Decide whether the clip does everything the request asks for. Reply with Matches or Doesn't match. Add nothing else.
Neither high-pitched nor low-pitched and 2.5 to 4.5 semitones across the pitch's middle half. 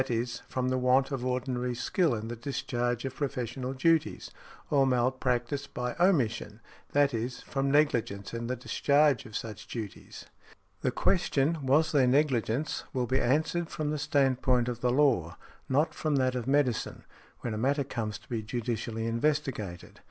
Doesn't match